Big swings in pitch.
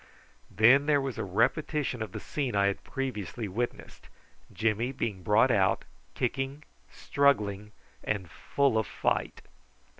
No: average, 4.8 semitones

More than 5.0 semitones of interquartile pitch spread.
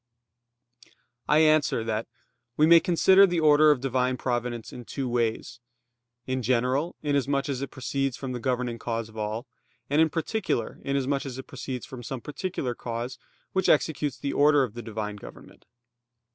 No: average, 3.5 semitones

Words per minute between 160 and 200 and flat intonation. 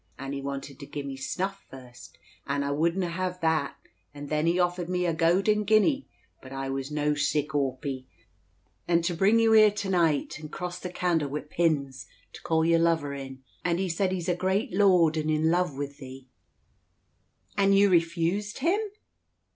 No: average, 185 wpm; average, 4.5 semitones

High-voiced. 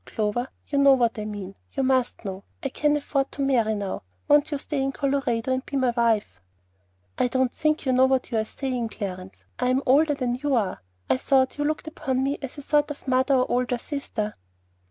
Yes: very high, 260 Hz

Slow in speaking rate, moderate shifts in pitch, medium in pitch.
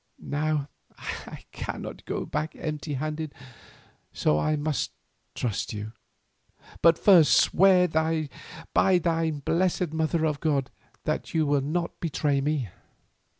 No: slow, 120 wpm; narrow, 2.3 semitones; medium, 155 Hz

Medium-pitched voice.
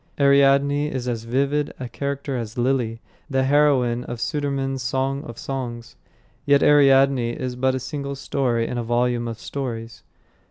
No: low, 130 Hz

